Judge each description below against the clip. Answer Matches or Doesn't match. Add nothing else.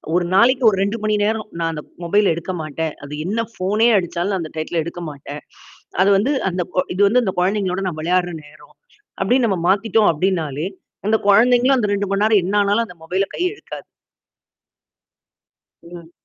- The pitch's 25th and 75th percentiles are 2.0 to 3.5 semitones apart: Doesn't match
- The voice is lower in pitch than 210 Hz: Matches